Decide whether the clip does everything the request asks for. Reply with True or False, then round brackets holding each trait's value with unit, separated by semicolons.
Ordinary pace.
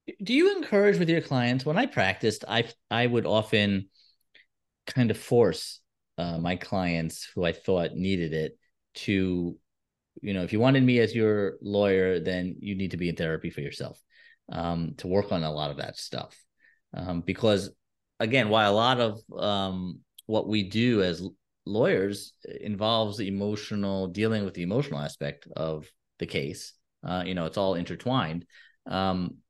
True (170 wpm)